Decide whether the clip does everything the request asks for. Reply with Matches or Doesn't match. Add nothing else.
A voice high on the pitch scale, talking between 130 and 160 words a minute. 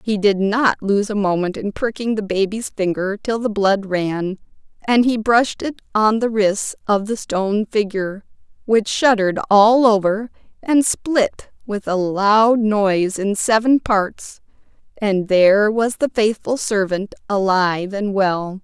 Matches